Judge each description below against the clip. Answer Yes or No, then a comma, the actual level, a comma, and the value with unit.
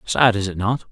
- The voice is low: Yes, low, 105 Hz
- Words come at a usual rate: No, fast, 260 wpm